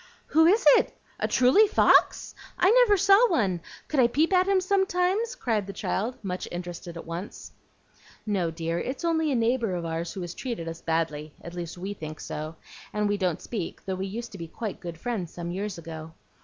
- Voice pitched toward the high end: Yes, high, 200 Hz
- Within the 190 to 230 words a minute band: Yes, average, 200 wpm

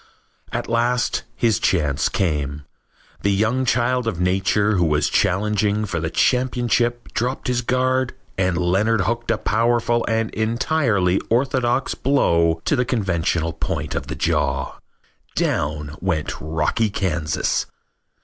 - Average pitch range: No, wide, 6.0 semitones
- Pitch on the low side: Yes, low, 105 Hz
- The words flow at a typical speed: No, slow, 130 wpm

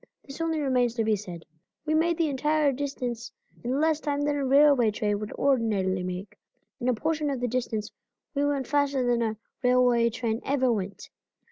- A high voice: Yes, very high, 250 Hz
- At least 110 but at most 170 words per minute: No, average, 190 wpm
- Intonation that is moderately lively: Yes, average, 4.3 semitones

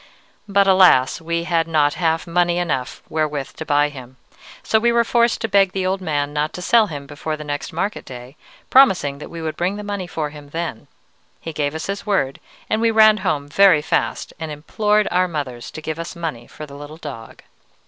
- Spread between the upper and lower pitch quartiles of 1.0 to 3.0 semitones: No, average, 4.7 semitones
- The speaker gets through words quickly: Yes, fast, 210 wpm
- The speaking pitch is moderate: Yes, medium, 160 Hz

